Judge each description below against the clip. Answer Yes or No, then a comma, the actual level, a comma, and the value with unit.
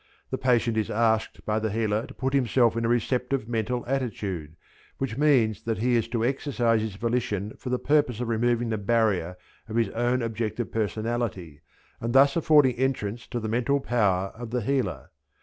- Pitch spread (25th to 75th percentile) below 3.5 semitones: Yes, narrow, 2.5 semitones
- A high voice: No, low, 115 Hz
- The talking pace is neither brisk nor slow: Yes, average, 185 wpm